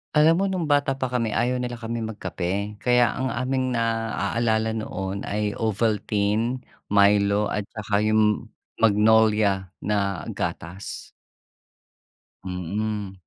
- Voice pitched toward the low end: Yes, low, 110 Hz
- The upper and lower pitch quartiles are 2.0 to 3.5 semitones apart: Yes, average, 2.7 semitones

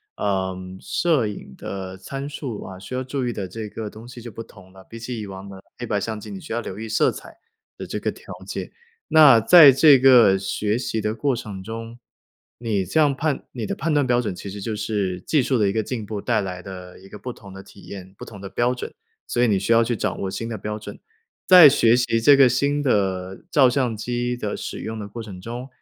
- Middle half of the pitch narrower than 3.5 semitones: No, average, 4.1 semitones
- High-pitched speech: No, low, 110 Hz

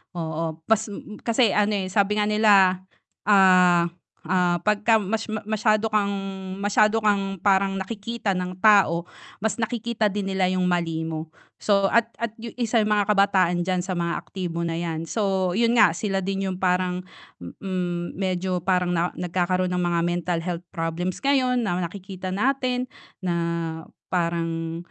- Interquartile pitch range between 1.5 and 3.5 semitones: Yes, average, 3.1 semitones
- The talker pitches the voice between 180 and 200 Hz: Yes, high, 190 Hz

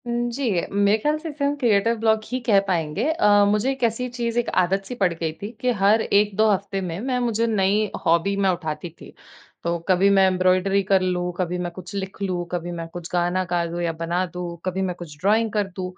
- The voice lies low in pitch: No, high, 195 Hz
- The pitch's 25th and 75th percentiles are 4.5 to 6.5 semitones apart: No, average, 3.9 semitones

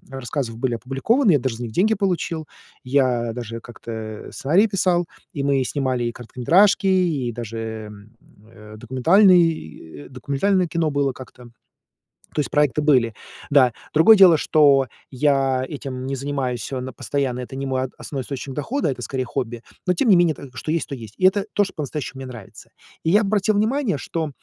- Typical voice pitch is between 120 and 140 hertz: Yes, low, 135 Hz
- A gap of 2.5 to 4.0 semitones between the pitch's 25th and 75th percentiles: No, average, 5.3 semitones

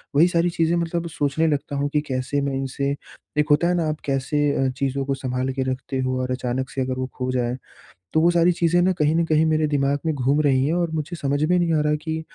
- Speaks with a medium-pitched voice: Yes, medium, 145 Hz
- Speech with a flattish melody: No, average, 3.3 semitones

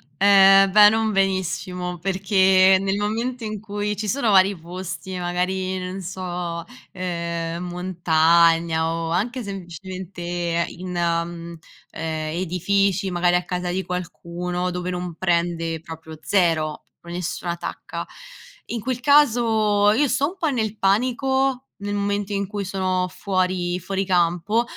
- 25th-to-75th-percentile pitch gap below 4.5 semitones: Yes, average, 2.7 semitones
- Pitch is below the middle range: No, medium, 185 Hz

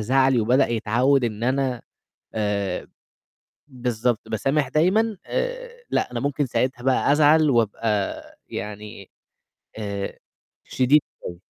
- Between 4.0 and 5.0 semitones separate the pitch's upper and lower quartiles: Yes, average, 4.6 semitones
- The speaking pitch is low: Yes, low, 125 Hz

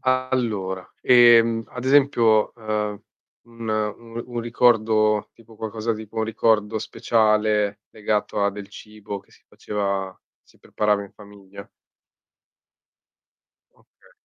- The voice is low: Yes, low, 110 Hz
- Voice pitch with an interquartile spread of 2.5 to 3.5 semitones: No, narrow, 1.9 semitones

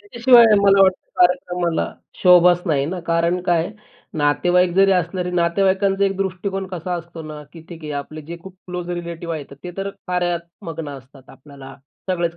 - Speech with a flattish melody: Yes, narrow, 2.2 semitones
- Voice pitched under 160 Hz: No, medium, 175 Hz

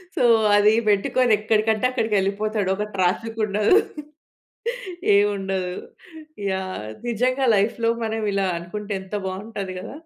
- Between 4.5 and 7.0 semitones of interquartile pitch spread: No, narrow, 2.5 semitones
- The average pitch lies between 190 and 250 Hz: Yes, high, 205 Hz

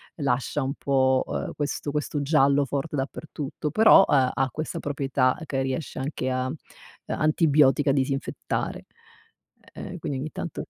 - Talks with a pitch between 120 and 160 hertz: Yes, medium, 140 Hz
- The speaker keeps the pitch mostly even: Yes, narrow, 2.0 semitones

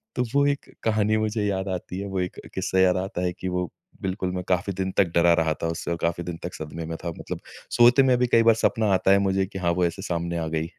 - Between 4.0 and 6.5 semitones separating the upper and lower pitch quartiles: No, average, 3.4 semitones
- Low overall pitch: Yes, very low, 95 Hz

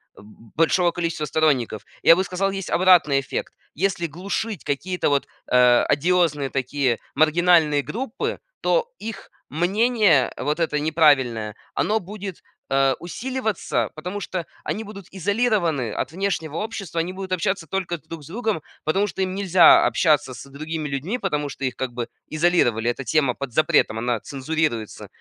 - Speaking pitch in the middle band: Yes, medium, 165 Hz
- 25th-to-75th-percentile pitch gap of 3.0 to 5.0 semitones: No, wide, 5.5 semitones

